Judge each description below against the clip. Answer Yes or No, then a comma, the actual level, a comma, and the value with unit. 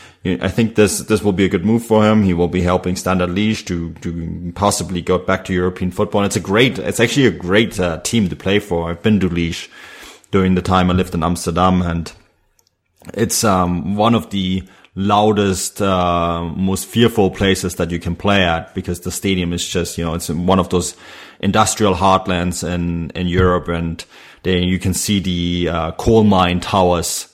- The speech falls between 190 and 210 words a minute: Yes, average, 200 wpm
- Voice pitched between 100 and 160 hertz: No, very low, 90 Hz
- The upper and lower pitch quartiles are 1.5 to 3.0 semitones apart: Yes, narrow, 2.5 semitones